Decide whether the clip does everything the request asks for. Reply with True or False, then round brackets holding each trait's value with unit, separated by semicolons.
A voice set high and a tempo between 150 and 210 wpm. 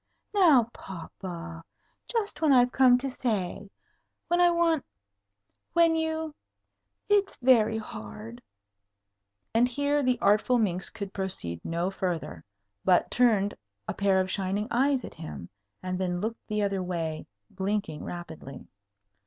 False (205 Hz; 135 wpm)